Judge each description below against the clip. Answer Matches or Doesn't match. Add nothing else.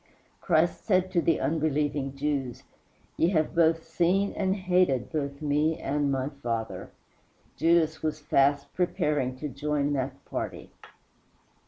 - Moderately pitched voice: Matches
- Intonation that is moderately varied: Matches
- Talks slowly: Matches